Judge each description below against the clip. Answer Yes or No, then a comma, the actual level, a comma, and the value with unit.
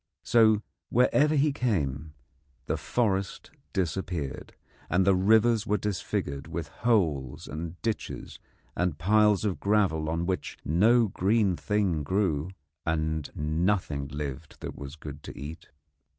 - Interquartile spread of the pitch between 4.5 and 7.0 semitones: Yes, wide, 5.5 semitones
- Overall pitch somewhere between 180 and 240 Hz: No, very low, 90 Hz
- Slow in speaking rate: Yes, slow, 125 wpm